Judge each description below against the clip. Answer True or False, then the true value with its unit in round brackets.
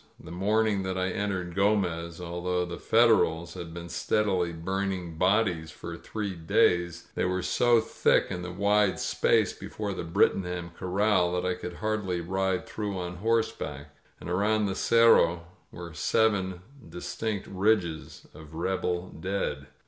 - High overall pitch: False (90 Hz)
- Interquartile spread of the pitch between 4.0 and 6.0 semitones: False (2.9 semitones)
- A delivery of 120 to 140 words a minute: False (155 wpm)